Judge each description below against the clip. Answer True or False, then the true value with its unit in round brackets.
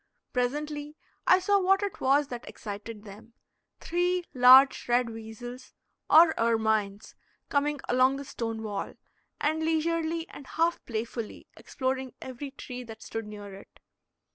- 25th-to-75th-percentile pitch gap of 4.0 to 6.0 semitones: True (5.2 semitones)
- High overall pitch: True (255 Hz)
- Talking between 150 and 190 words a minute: False (135 wpm)